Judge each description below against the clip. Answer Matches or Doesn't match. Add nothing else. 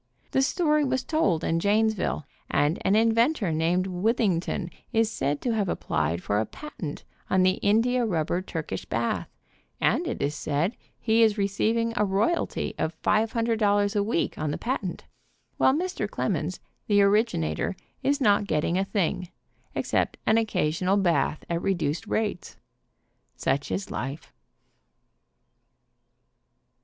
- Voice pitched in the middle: Doesn't match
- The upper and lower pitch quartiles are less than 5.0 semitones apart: Doesn't match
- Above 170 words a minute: Doesn't match